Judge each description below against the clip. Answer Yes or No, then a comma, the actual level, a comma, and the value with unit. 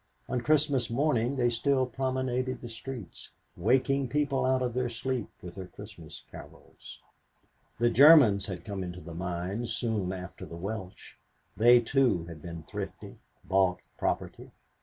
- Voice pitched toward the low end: Yes, low, 120 Hz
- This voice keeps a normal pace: Yes, average, 145 wpm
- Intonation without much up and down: No, wide, 5.5 semitones